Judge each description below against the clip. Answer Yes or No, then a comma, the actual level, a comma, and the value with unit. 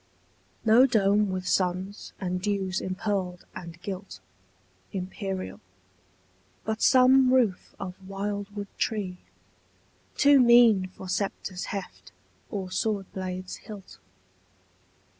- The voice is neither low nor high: No, high, 195 Hz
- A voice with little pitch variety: Yes, narrow, 2.3 semitones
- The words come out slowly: Yes, slow, 95 wpm